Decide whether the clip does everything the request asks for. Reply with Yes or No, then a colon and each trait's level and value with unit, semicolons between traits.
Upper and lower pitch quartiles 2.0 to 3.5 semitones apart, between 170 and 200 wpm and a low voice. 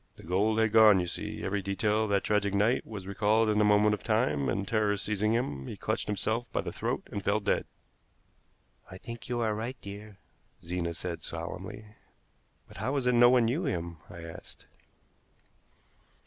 Yes: average, 2.9 semitones; average, 190 wpm; low, 105 Hz